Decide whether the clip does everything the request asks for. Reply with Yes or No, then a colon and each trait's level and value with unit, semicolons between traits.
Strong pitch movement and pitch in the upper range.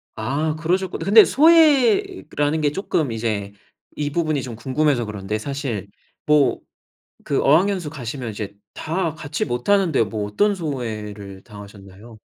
No: wide, 7.2 semitones; medium, 140 Hz